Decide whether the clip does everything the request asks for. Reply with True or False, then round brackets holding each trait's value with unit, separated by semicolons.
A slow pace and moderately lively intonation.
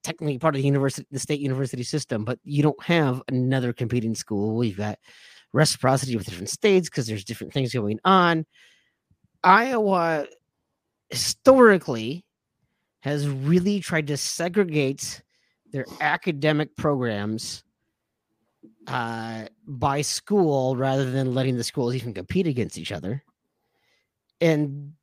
True (125 wpm; 4.4 semitones)